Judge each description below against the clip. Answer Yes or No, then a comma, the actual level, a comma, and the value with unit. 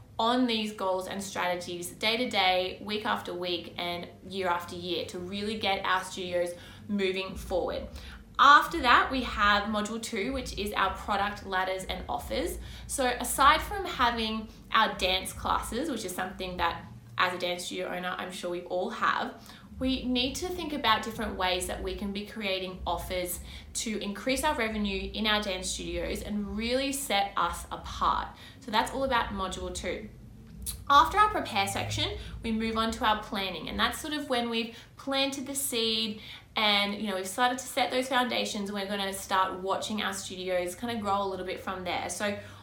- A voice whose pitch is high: Yes, high, 205 Hz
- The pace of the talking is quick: No, average, 185 wpm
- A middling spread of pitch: Yes, average, 4.0 semitones